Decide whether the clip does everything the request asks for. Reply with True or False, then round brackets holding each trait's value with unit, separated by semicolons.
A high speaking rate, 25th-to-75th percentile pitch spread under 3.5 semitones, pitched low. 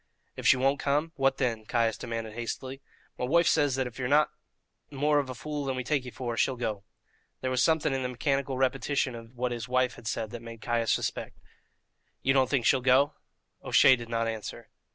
True (215 wpm; 2.5 semitones; 130 Hz)